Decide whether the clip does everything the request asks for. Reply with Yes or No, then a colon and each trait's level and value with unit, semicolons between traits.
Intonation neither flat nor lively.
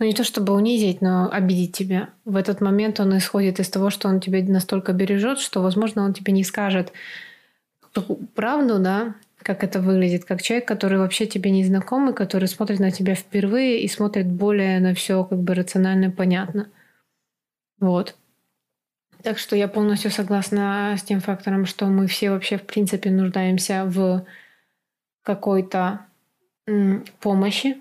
No: narrow, 1.7 semitones